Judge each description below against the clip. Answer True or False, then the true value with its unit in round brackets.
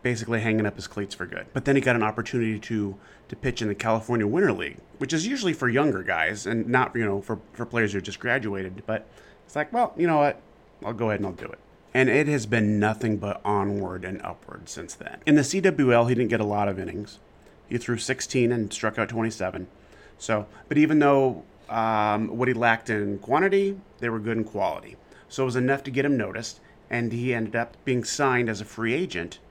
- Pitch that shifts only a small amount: False (3.4 semitones)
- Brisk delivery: True (230 wpm)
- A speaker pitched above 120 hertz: False (115 Hz)